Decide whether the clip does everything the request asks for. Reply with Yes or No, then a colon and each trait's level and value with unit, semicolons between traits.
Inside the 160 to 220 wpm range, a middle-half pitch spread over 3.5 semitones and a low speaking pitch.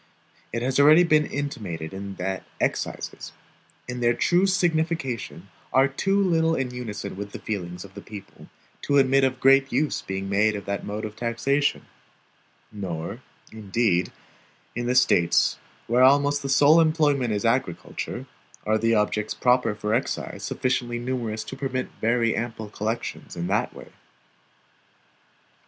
No: average, 145 wpm; average, 4.7 semitones; low, 120 Hz